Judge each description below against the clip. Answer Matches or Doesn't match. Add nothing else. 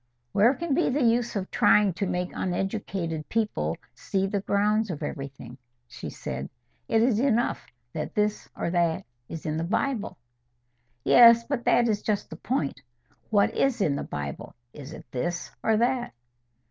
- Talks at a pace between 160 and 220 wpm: Matches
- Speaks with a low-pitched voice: Doesn't match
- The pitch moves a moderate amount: Doesn't match